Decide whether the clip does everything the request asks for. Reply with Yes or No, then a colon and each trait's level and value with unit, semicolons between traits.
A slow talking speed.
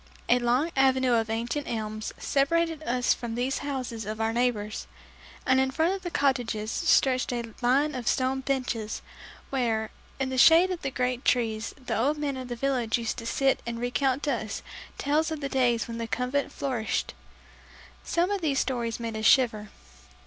No: average, 185 wpm